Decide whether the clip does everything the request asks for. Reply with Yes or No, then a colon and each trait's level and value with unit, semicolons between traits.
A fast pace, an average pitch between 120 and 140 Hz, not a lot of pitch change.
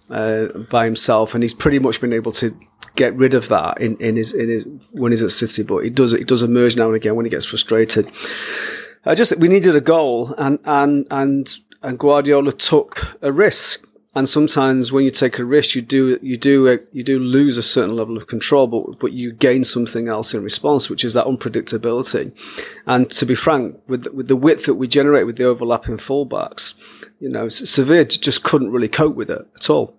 No: fast, 220 wpm; low, 125 Hz; average, 3.1 semitones